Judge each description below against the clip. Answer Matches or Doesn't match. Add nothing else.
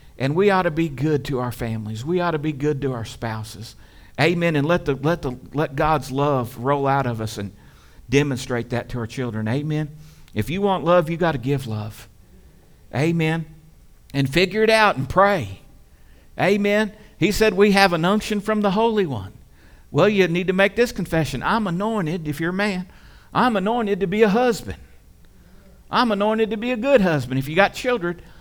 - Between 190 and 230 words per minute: Matches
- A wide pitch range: Matches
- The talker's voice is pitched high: Doesn't match